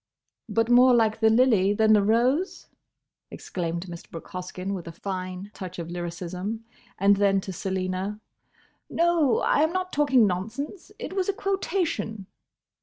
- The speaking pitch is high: Yes, high, 210 Hz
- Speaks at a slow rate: No, average, 150 wpm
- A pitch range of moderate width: No, wide, 5.9 semitones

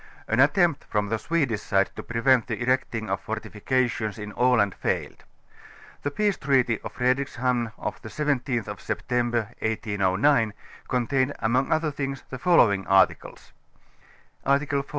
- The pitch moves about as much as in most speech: Yes, average, 4.0 semitones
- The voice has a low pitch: Yes, low, 125 Hz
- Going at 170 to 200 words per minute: No, average, 140 wpm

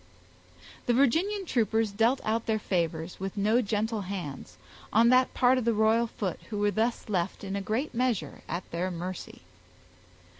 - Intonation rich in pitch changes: No, average, 3.7 semitones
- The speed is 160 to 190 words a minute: Yes, average, 165 wpm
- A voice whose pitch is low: No, high, 215 Hz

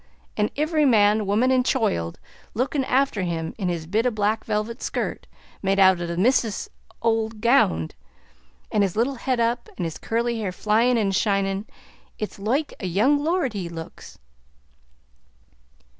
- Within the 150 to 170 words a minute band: Yes, average, 160 wpm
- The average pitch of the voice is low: No, high, 215 Hz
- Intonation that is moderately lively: Yes, average, 4.2 semitones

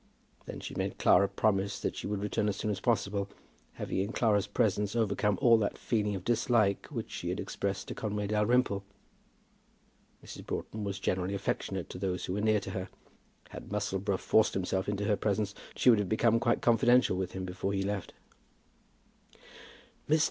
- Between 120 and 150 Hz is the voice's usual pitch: No, low, 100 Hz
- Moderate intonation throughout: No, narrow, 1.9 semitones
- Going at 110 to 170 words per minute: No, average, 185 wpm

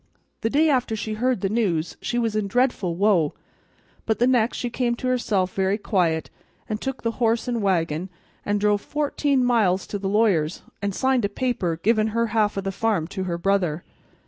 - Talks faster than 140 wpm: Yes, average, 200 wpm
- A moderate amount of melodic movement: Yes, average, 4.0 semitones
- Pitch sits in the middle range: No, high, 215 Hz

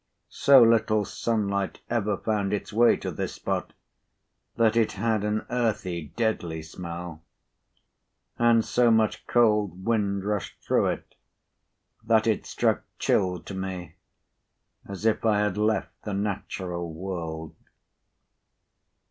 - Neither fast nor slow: No, slow, 125 wpm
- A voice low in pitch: Yes, low, 105 Hz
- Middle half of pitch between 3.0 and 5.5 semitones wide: Yes, average, 3.3 semitones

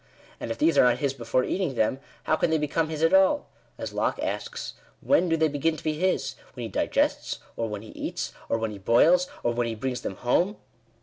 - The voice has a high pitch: No, medium, 140 Hz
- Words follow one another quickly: Yes, fast, 240 wpm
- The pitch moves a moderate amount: No, wide, 5.8 semitones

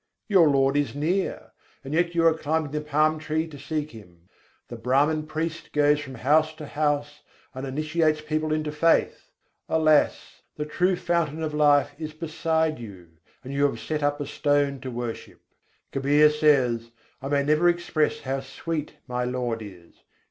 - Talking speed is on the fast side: No, average, 165 wpm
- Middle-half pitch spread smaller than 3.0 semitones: Yes, narrow, 2.4 semitones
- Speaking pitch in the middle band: Yes, medium, 150 Hz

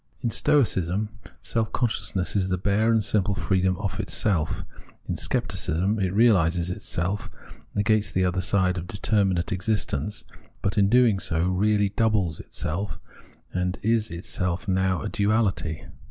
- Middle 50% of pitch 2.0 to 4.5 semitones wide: Yes, average, 2.8 semitones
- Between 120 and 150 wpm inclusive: Yes, average, 140 wpm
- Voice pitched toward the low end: Yes, very low, 95 Hz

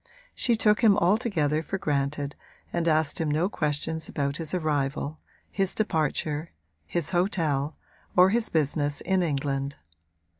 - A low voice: No, medium, 155 Hz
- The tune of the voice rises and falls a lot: No, average, 4.1 semitones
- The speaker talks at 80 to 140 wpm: Yes, slow, 135 wpm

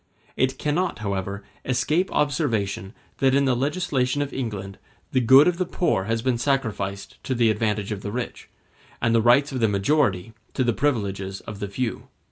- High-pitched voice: No, low, 120 Hz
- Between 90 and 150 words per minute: No, average, 180 wpm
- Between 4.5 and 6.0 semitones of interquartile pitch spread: Yes, average, 5.2 semitones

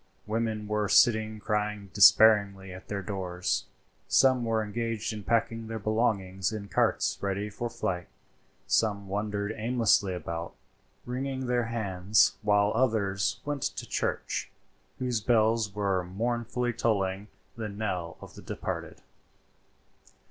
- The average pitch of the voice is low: Yes, low, 105 Hz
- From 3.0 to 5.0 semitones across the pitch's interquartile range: No, narrow, 2.6 semitones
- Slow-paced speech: Yes, slow, 125 wpm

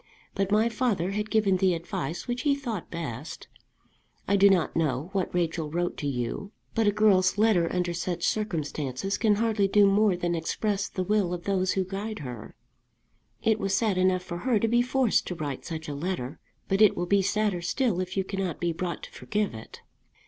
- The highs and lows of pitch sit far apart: No, average, 3.5 semitones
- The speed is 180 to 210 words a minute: Yes, average, 200 wpm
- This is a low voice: No, high, 190 Hz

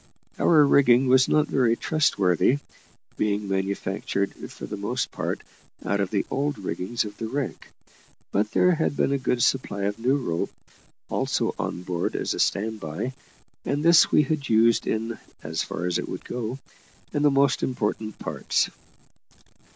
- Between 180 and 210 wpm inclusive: No, average, 165 wpm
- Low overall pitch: Yes, low, 115 Hz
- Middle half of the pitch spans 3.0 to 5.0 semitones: No, wide, 5.5 semitones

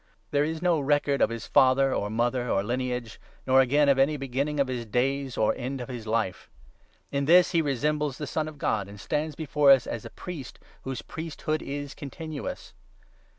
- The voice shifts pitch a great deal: No, average, 3.3 semitones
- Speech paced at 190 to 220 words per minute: Yes, average, 195 wpm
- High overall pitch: No, low, 135 Hz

